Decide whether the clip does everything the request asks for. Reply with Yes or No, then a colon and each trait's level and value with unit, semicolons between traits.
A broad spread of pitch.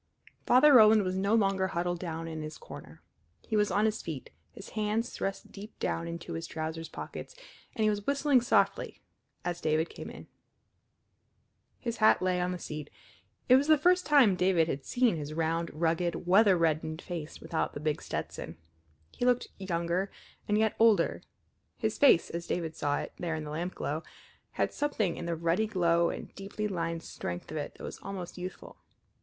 No: average, 4.5 semitones